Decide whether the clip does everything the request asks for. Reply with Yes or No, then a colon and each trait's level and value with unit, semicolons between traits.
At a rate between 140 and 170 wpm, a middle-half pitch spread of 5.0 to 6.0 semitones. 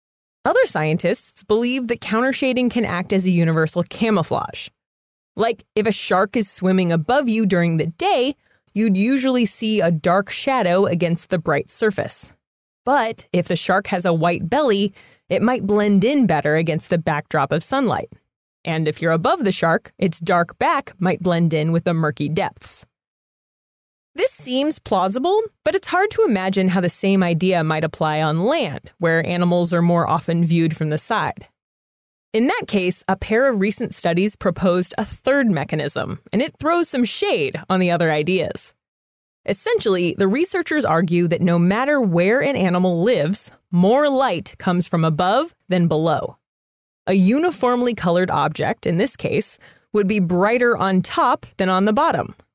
Yes: average, 165 wpm; wide, 5.5 semitones